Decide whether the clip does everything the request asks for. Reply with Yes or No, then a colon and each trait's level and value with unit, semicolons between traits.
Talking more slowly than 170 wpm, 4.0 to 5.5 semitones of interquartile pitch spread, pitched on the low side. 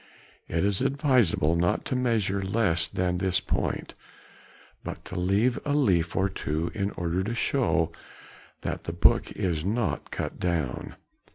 Yes: average, 150 wpm; average, 5.2 semitones; very low, 95 Hz